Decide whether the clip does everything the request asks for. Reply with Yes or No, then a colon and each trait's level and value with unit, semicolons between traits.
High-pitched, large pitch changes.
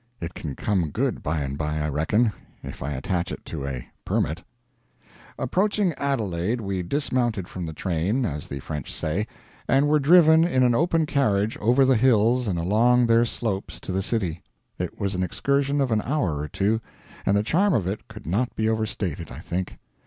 No: low, 105 Hz; wide, 7.1 semitones